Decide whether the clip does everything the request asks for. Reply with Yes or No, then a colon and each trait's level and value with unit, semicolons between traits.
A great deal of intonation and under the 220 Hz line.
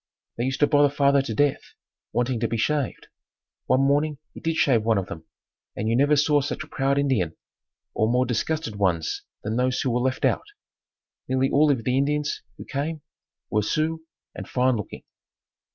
No: average, 3.9 semitones; low, 135 Hz